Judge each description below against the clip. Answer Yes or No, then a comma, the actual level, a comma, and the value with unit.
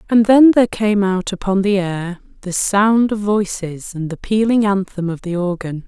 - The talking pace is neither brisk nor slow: Yes, average, 195 wpm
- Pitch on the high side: Yes, high, 195 Hz